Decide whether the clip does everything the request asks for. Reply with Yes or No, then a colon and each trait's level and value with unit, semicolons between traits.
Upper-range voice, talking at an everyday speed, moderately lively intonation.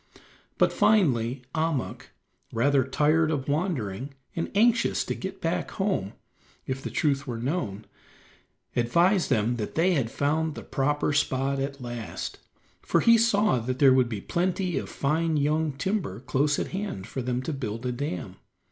No: medium, 140 Hz; average, 160 wpm; average, 4.8 semitones